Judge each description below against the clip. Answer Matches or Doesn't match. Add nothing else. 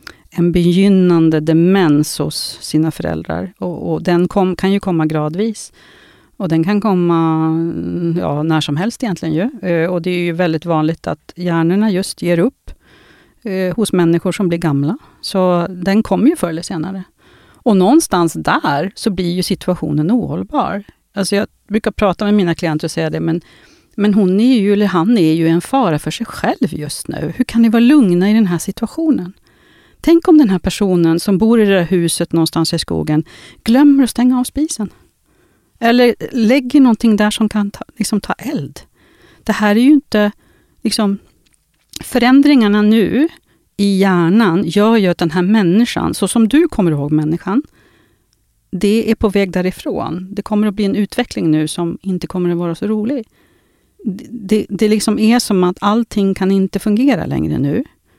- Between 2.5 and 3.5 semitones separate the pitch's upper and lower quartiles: Doesn't match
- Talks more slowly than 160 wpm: Doesn't match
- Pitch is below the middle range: Doesn't match